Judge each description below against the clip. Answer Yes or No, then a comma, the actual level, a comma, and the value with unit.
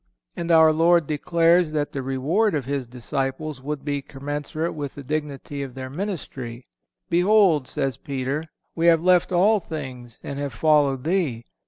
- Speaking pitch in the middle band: Yes, medium, 150 Hz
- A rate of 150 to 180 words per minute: Yes, average, 160 wpm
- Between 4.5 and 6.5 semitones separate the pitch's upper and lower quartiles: No, average, 3.7 semitones